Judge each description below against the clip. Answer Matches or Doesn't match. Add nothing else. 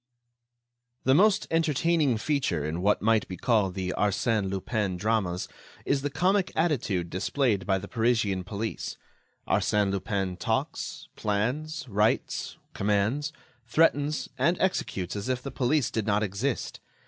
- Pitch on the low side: Matches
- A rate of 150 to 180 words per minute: Doesn't match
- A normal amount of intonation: Doesn't match